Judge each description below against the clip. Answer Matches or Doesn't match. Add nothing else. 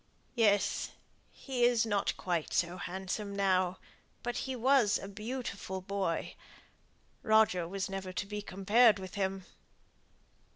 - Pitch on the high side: Matches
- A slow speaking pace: Matches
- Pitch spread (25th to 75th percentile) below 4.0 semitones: Matches